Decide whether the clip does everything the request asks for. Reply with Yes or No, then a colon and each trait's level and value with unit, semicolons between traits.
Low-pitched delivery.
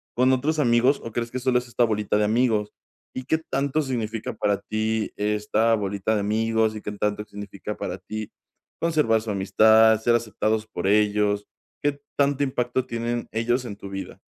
Yes: low, 110 Hz